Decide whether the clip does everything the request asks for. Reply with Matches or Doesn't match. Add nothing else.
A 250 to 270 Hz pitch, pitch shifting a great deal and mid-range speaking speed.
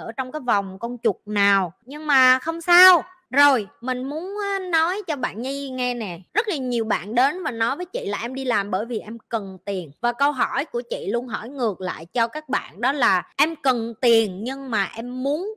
Matches